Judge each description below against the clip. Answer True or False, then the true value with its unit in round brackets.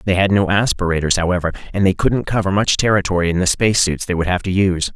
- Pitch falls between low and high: False (95 Hz)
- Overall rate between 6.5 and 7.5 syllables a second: True (6.7 syllables/s)